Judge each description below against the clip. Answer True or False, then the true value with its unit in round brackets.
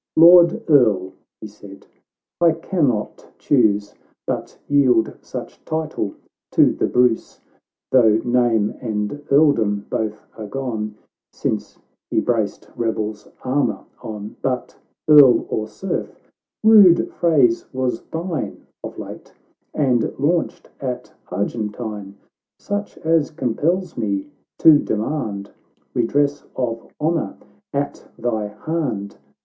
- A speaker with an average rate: False (120 wpm)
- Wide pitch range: True (6.0 semitones)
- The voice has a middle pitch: False (125 Hz)